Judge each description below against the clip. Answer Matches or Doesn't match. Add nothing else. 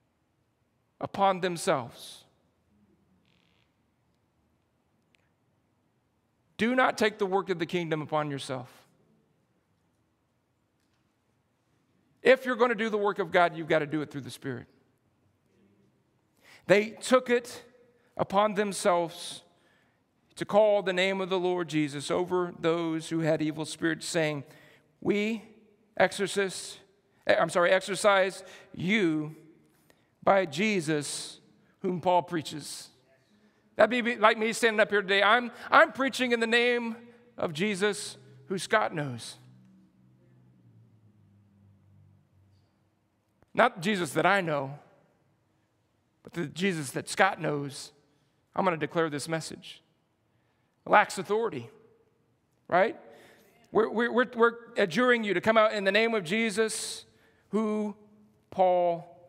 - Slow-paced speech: Matches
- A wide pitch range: Matches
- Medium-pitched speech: Matches